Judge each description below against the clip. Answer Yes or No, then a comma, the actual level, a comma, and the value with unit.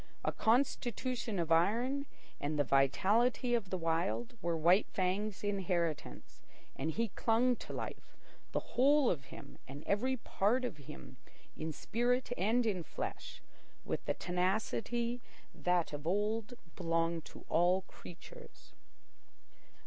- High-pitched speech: Yes, high, 195 Hz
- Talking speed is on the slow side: Yes, slow, 130 wpm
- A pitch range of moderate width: No, wide, 6.2 semitones